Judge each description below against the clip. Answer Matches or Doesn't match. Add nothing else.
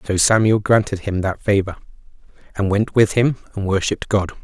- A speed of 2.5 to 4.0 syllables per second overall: Doesn't match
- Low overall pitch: Matches